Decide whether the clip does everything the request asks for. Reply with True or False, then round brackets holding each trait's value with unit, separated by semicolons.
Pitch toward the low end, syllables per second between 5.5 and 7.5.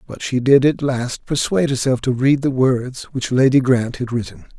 False (130 Hz; 4.9 syllables/s)